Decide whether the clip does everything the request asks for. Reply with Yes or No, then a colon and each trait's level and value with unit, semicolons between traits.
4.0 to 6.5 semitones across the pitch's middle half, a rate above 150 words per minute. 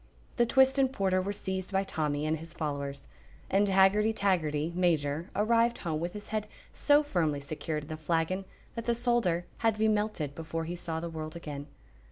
Yes: average, 5.2 semitones; average, 195 wpm